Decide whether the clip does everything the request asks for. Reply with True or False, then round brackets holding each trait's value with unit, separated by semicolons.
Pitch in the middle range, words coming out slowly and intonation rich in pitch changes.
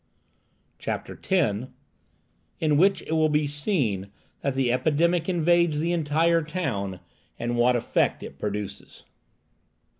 True (150 Hz; 120 wpm; 5.9 semitones)